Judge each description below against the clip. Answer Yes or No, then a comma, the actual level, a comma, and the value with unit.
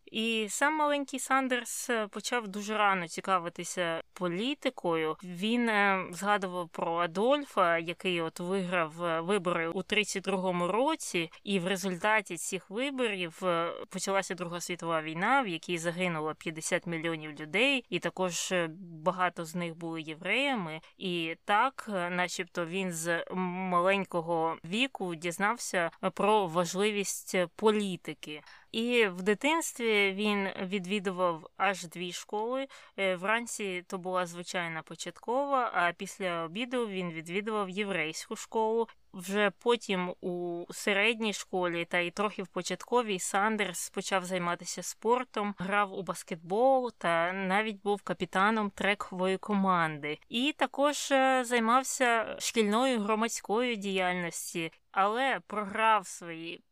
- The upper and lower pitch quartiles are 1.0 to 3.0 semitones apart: No, average, 3.7 semitones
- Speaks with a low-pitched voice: No, high, 195 Hz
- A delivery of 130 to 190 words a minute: No, average, 110 wpm